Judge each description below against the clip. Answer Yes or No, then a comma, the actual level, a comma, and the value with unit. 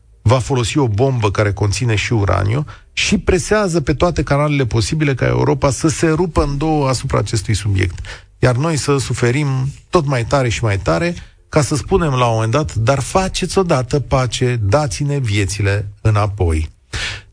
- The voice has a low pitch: Yes, low, 125 Hz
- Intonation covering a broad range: Yes, wide, 6.1 semitones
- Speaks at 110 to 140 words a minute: No, average, 165 wpm